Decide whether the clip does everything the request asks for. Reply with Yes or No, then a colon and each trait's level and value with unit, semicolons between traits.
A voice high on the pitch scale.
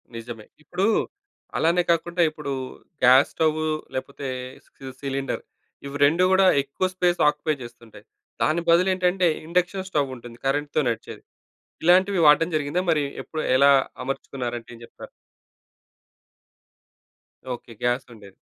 No: medium, 150 Hz